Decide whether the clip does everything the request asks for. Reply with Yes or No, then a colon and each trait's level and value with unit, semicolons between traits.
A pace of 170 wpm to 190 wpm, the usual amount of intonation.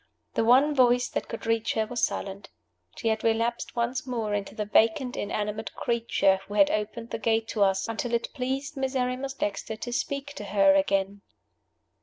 Yes: average, 180 wpm; average, 3.2 semitones